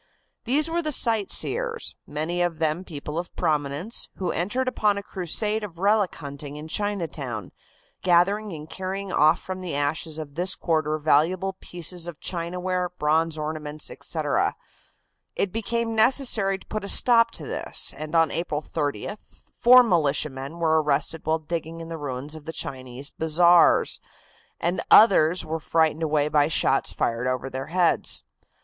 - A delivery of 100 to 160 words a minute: Yes, average, 155 wpm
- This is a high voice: No, medium, 165 Hz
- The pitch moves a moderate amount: Yes, average, 4.2 semitones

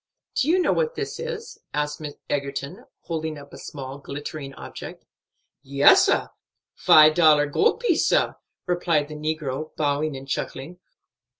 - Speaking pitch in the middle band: Yes, medium, 150 Hz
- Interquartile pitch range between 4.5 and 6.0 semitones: No, average, 3.2 semitones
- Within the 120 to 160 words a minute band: Yes, average, 140 wpm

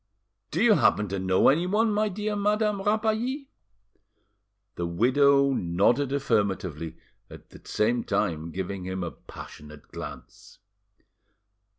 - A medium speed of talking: No, slow, 115 wpm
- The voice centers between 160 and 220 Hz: No, low, 120 Hz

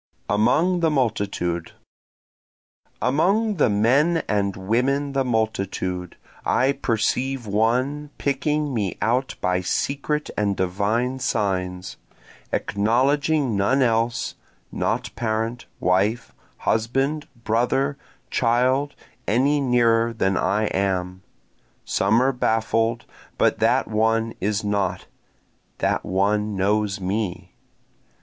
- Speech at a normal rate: No, slow, 100 wpm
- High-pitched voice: No, low, 115 Hz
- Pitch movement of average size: Yes, average, 4.9 semitones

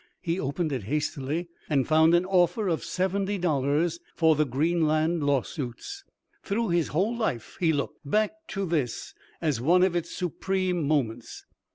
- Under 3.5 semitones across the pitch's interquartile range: No, average, 4.0 semitones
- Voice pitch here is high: No, medium, 165 Hz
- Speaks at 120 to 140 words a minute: No, average, 155 wpm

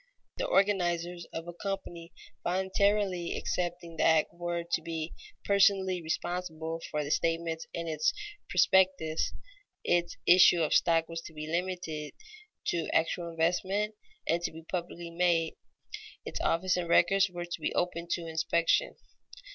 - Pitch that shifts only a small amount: Yes, narrow, 1.8 semitones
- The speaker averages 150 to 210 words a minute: No, average, 140 wpm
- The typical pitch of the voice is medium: Yes, medium, 170 Hz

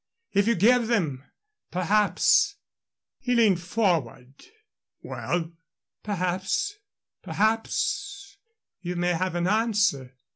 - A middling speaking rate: No, slow, 100 wpm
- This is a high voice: Yes, high, 200 Hz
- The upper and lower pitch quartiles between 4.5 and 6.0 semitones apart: Yes, average, 4.8 semitones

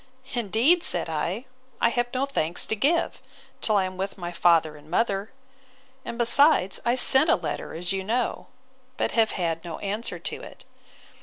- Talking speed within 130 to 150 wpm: No, average, 175 wpm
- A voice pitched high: Yes, high, 205 Hz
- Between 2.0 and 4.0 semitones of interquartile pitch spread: No, wide, 5.6 semitones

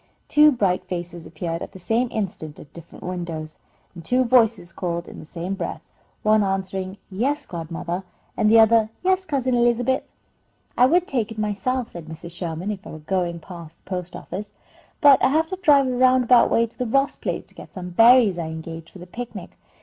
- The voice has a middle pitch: No, high, 195 Hz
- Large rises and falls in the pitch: Yes, wide, 6.2 semitones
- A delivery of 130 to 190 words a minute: No, average, 200 wpm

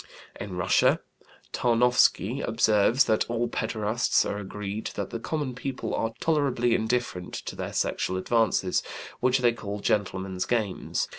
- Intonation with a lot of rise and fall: No, average, 3.4 semitones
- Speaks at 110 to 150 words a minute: Yes, slow, 135 wpm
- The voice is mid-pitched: No, low, 115 Hz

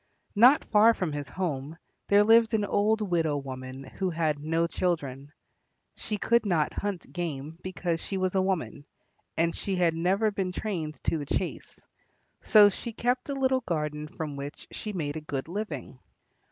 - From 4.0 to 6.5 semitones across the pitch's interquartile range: Yes, average, 5.3 semitones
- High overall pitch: No, medium, 175 Hz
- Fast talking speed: No, average, 175 wpm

